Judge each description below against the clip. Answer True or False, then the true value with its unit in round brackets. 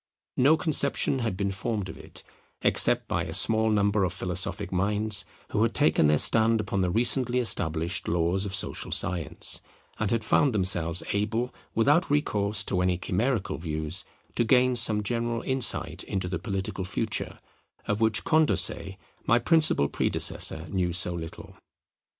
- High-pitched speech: False (100 Hz)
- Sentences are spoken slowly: False (155 wpm)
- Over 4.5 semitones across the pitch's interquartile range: False (4.2 semitones)